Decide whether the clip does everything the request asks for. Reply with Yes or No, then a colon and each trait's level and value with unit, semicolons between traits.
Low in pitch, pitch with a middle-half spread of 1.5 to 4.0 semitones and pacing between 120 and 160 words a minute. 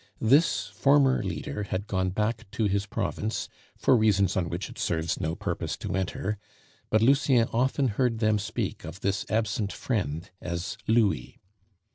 Yes: low, 105 Hz; average, 3.3 semitones; average, 155 wpm